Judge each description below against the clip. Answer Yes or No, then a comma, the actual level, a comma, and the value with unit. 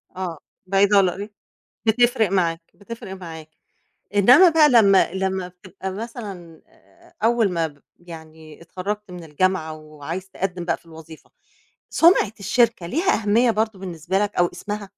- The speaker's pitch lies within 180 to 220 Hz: Yes, high, 190 Hz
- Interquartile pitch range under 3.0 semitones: No, average, 3.8 semitones